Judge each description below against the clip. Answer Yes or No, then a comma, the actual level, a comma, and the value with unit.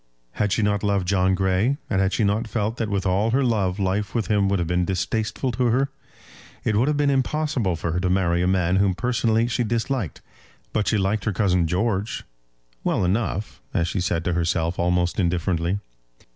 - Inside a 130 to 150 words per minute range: No, average, 200 wpm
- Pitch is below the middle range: Yes, low, 100 Hz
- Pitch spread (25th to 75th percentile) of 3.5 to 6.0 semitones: Yes, average, 3.8 semitones